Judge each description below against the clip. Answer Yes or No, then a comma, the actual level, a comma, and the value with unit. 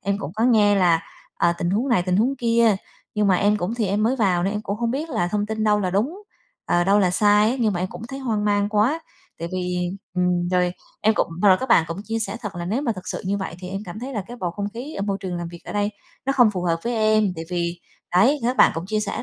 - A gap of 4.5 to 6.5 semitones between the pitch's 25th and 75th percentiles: No, average, 3.8 semitones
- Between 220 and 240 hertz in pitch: No, high, 205 Hz